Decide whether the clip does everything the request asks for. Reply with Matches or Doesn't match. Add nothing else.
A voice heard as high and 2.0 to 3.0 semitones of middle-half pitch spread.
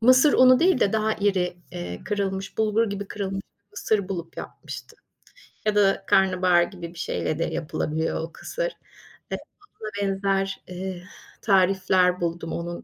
Matches